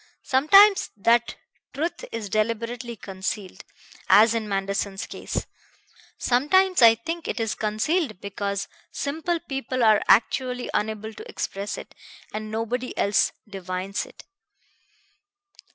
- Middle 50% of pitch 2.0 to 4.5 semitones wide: Yes, average, 4.2 semitones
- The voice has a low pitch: No, high, 225 Hz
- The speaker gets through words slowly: Yes, slow, 115 wpm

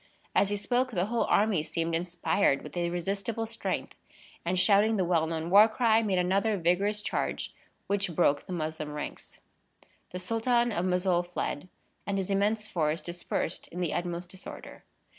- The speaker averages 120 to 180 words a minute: Yes, average, 160 wpm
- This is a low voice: No, medium, 185 Hz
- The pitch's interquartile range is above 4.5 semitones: No, average, 3.4 semitones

